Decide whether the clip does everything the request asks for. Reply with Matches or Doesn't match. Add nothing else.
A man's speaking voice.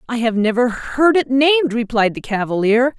Doesn't match